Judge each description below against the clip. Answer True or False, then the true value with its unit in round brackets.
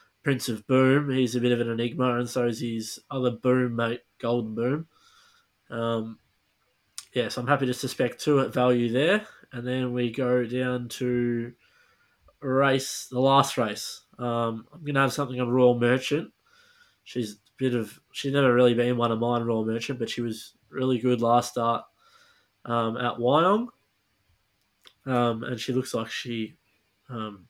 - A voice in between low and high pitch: False (125 Hz)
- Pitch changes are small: True (2.3 semitones)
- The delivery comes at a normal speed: True (170 wpm)